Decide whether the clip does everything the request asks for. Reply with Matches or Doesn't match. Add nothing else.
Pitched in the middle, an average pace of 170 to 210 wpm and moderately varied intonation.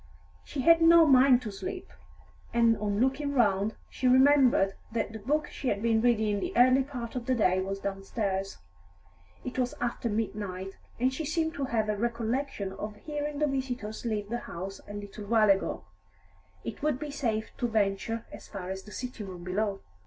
Doesn't match